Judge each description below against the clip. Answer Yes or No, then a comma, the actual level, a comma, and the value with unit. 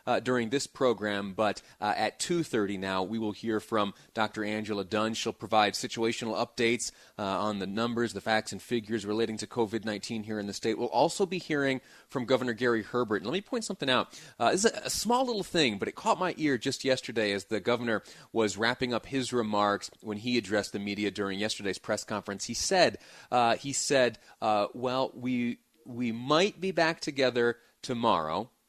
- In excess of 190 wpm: Yes, average, 200 wpm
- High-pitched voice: No, low, 115 Hz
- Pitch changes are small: No, average, 3.2 semitones